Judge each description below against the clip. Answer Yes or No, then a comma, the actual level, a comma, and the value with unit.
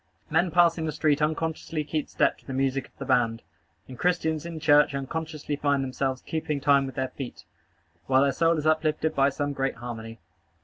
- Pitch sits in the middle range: Yes, medium, 145 Hz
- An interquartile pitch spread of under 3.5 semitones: Yes, average, 2.9 semitones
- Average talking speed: Yes, average, 190 wpm